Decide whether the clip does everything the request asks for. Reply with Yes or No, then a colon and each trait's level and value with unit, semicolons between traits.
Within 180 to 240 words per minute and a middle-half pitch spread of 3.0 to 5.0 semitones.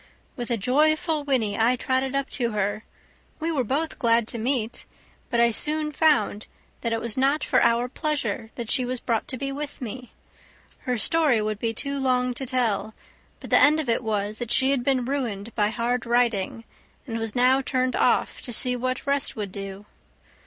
Yes: average, 195 wpm; average, 3.3 semitones